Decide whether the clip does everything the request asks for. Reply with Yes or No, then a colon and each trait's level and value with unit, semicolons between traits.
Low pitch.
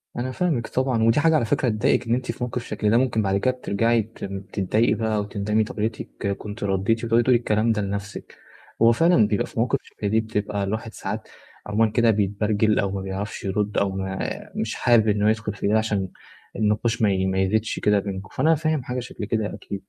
Yes: low, 110 Hz